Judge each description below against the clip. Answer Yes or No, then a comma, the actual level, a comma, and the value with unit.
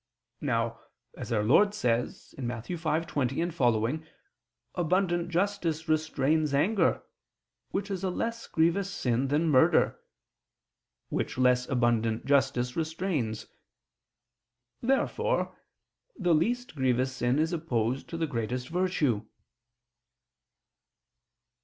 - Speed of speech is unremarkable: No, slow, 100 wpm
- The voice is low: No, medium, 155 Hz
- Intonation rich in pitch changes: Yes, wide, 6.0 semitones